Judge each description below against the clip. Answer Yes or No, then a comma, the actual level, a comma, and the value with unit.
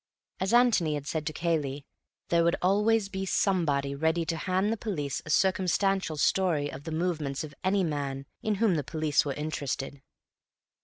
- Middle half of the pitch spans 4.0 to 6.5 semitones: Yes, average, 4.7 semitones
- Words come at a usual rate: Yes, average, 170 wpm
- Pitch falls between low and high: Yes, medium, 165 Hz